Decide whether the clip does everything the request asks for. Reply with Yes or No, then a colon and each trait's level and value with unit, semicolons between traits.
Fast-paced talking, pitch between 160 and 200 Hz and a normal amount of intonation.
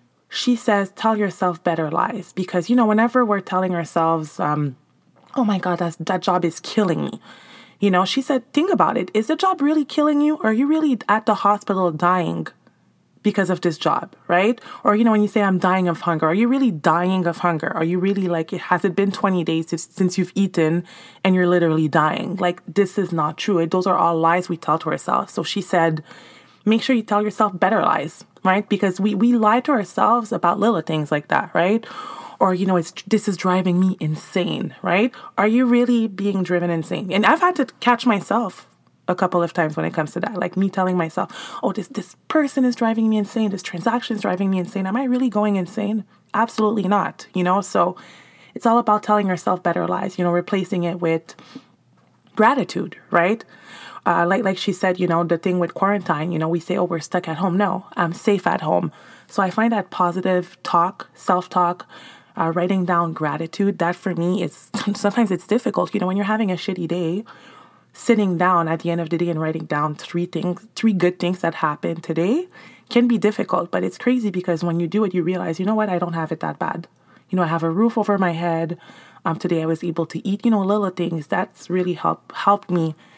Yes: fast, 225 wpm; medium, 185 Hz; average, 3.7 semitones